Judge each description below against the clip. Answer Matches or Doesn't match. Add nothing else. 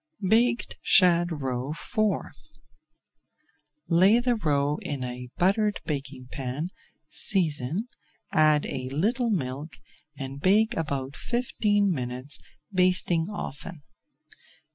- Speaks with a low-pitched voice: Doesn't match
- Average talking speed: Doesn't match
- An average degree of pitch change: Doesn't match